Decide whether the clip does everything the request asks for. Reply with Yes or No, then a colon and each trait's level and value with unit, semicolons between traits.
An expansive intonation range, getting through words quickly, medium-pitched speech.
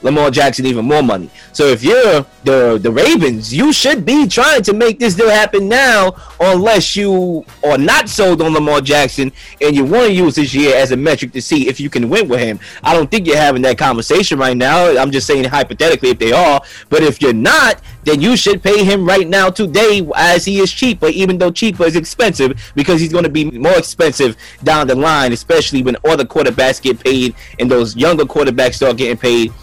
Yes: wide, 7.3 semitones; fast, 215 wpm; medium, 155 Hz